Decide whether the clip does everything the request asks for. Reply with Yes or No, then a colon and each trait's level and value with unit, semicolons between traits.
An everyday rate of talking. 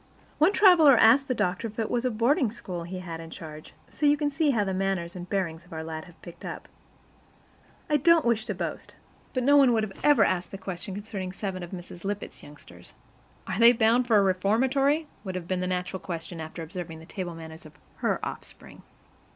No: fast, 220 wpm